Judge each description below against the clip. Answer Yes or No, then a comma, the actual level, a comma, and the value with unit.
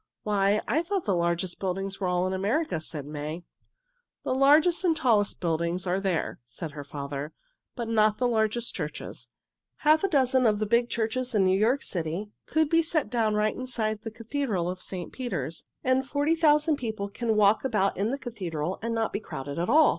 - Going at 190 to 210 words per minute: Yes, average, 200 wpm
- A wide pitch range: Yes, wide, 6.0 semitones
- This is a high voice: Yes, high, 215 Hz